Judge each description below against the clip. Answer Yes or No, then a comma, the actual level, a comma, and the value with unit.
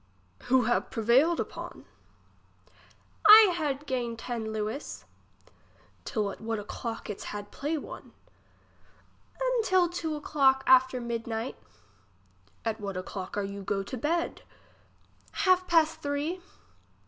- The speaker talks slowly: Yes, slow, 125 wpm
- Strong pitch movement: Yes, wide, 6.4 semitones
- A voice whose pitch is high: Yes, very high, 260 Hz